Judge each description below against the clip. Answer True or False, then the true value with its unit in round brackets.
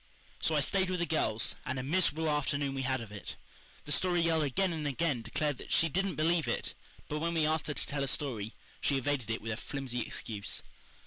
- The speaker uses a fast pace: True (235 wpm)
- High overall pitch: False (145 Hz)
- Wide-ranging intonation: False (4.1 semitones)